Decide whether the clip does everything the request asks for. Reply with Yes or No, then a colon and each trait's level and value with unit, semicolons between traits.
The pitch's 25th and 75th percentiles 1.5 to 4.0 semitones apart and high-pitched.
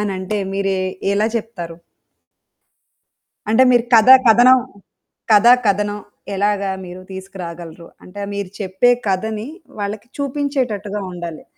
Yes: average, 2.9 semitones; high, 205 Hz